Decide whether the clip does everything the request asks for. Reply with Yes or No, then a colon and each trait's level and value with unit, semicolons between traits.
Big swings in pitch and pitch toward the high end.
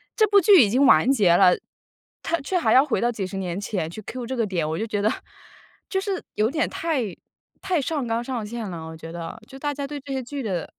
Yes: wide, 6.7 semitones; high, 235 Hz